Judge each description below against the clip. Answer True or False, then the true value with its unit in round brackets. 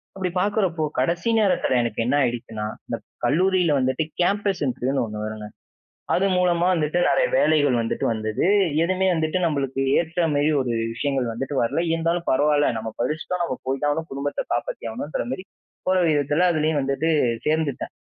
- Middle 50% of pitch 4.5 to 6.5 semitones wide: True (4.8 semitones)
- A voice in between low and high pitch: True (150 Hz)